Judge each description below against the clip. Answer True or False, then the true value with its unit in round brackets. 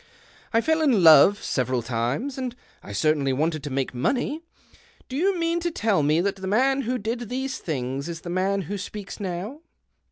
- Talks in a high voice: True (200 Hz)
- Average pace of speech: True (190 wpm)